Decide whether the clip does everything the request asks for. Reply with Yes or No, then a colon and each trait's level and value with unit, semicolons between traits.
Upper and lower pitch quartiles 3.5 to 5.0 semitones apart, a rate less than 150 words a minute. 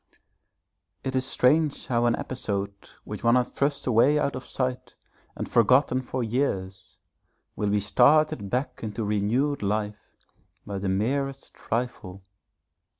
Yes: average, 4.2 semitones; slow, 135 wpm